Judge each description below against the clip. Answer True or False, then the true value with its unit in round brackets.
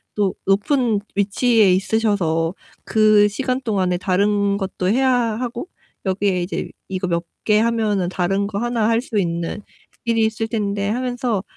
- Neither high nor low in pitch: False (205 Hz)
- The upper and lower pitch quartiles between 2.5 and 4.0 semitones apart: True (3.0 semitones)